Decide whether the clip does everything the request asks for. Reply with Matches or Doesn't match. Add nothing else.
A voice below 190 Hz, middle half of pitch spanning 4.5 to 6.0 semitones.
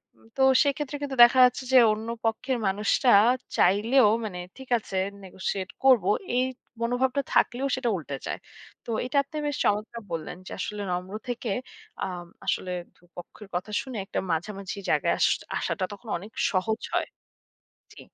Doesn't match